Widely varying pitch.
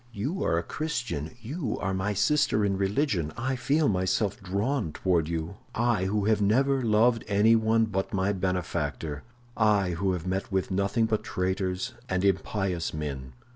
No: average, 3.7 semitones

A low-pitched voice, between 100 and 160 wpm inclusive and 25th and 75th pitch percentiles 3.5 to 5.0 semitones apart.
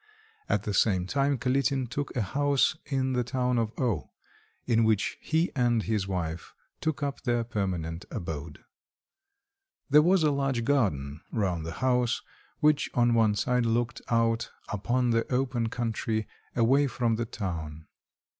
Yes: low, 120 Hz; average, 150 wpm; average, 4.1 semitones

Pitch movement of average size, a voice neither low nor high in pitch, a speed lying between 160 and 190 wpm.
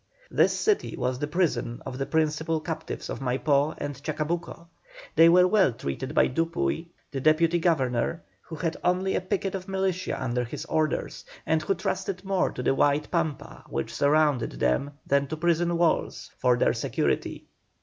Yes: average, 3.9 semitones; medium, 160 Hz; average, 170 wpm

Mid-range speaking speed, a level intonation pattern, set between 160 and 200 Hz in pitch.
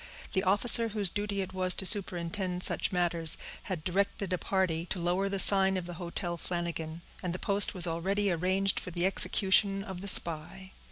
Yes: average, 185 wpm; narrow, 2.3 semitones; medium, 185 Hz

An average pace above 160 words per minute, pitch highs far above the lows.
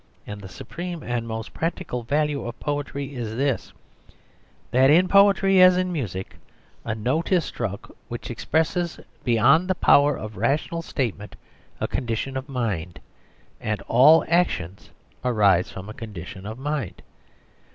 No: average, 140 wpm; wide, 6.7 semitones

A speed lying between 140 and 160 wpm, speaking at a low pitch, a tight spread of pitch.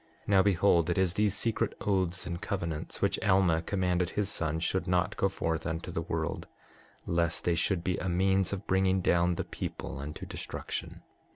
No: average, 185 wpm; very low, 90 Hz; narrow, 2.3 semitones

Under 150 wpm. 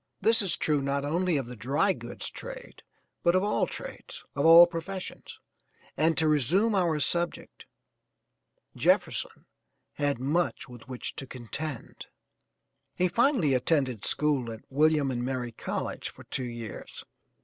Yes: average, 140 wpm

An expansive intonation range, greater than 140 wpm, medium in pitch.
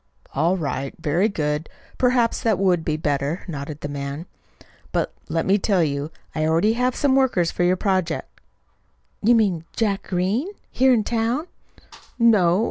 Yes: wide, 6.3 semitones; average, 155 wpm; medium, 180 Hz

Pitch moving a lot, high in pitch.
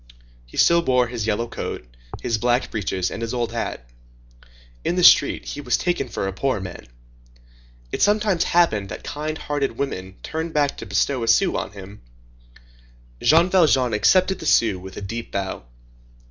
No: wide, 7.4 semitones; low, 120 Hz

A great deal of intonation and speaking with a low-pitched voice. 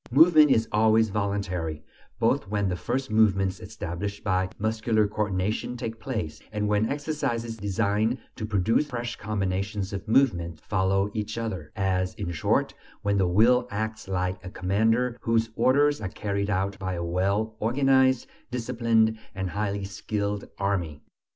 No: average, 3.0 semitones; low, 105 Hz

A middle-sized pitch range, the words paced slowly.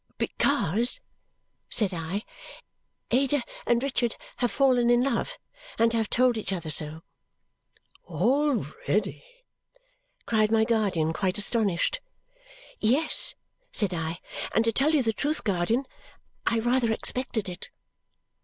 Yes: average, 4.5 semitones; slow, 115 wpm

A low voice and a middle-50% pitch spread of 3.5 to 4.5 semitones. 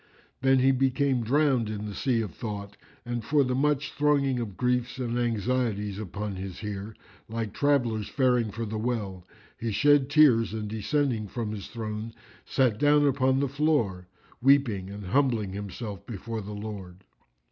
Yes: low, 115 Hz; average, 4.2 semitones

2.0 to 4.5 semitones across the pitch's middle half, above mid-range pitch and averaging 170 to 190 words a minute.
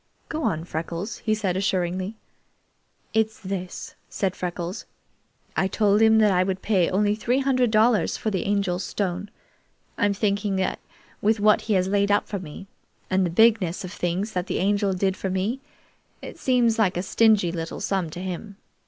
Yes: average, 2.8 semitones; high, 195 Hz; average, 180 wpm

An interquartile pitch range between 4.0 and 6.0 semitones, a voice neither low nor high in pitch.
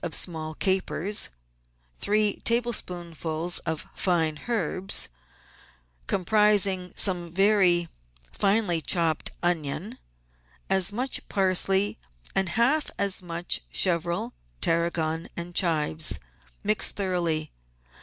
No: average, 3.1 semitones; medium, 180 Hz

